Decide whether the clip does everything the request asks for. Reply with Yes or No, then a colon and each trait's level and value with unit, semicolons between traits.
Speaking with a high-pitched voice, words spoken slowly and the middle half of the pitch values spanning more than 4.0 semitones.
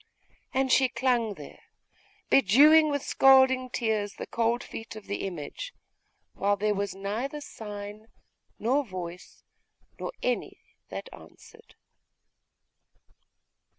Yes: high, 230 Hz; slow, 110 wpm; average, 4.7 semitones